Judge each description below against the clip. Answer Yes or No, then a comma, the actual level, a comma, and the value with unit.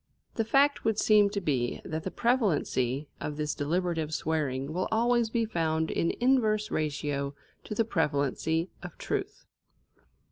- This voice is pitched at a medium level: Yes, medium, 165 Hz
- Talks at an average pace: Yes, average, 145 wpm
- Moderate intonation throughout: No, wide, 6.6 semitones